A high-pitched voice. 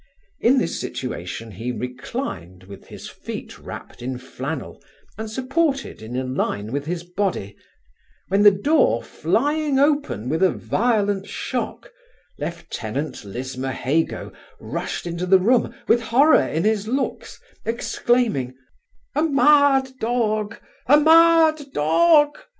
Yes: high, 205 Hz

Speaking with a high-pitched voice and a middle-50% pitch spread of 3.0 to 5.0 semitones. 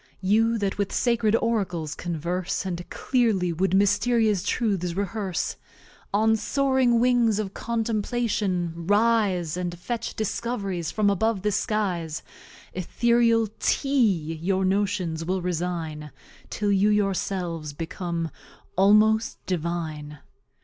Yes: high, 195 Hz; average, 4.2 semitones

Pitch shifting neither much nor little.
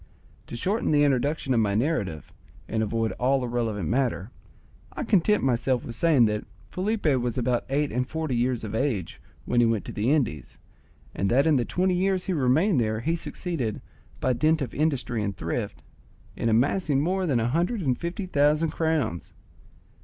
No: wide, 5.7 semitones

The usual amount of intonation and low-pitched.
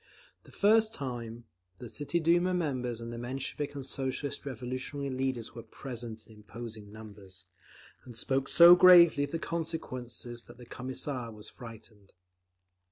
Yes: average, 3.9 semitones; low, 130 Hz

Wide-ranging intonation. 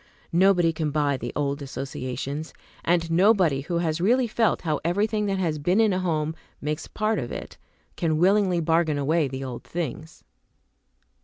No: average, 4.2 semitones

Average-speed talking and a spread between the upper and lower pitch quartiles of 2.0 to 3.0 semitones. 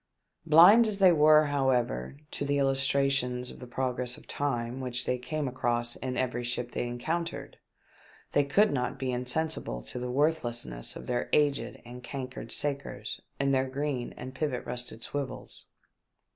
Yes: average, 160 wpm; average, 2.7 semitones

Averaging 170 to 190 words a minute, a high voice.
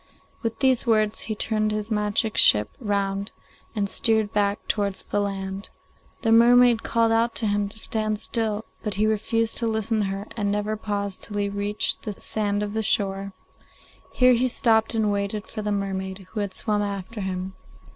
Yes: average, 185 wpm; high, 210 Hz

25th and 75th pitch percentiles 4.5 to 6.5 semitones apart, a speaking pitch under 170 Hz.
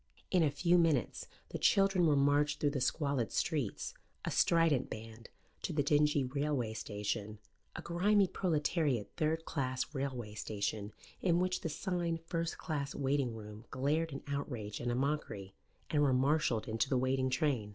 Yes: average, 5.0 semitones; medium, 140 Hz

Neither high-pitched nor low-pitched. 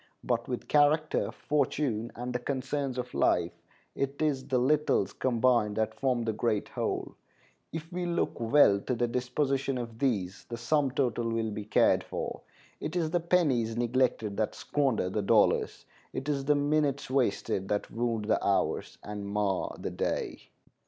No: low, 125 Hz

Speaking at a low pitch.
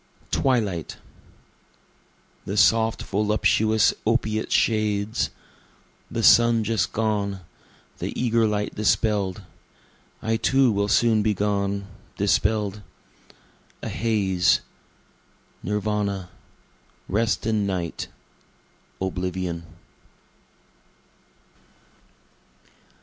Yes: low, 105 Hz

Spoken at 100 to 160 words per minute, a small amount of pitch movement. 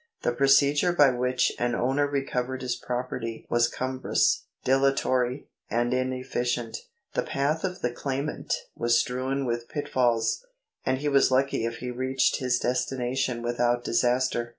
Yes: average, 145 wpm; narrow, 1.8 semitones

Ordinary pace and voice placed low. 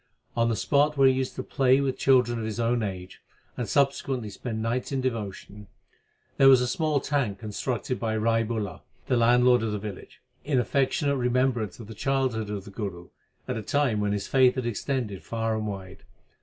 Yes: average, 195 wpm; low, 120 Hz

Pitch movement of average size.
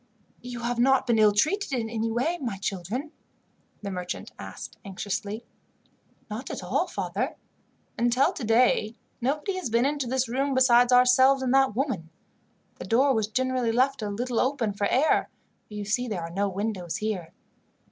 Yes: average, 3.8 semitones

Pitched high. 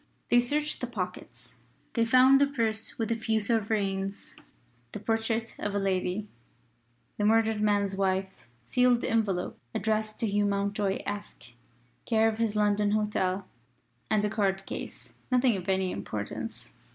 Yes: high, 210 Hz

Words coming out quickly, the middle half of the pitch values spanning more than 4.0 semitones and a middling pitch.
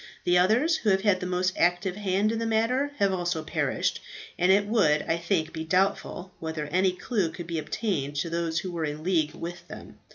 No: fast, 215 wpm; average, 3.6 semitones; medium, 180 Hz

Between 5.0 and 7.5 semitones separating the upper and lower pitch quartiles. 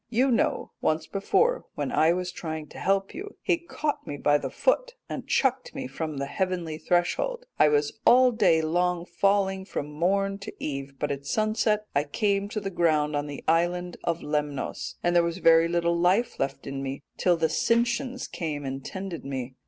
Yes: wide, 5.6 semitones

